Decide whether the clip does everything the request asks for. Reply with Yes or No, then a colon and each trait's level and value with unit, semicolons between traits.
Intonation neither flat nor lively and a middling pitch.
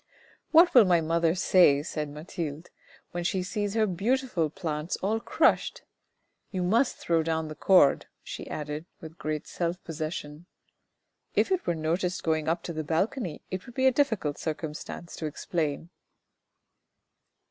Yes: average, 3.6 semitones; medium, 170 Hz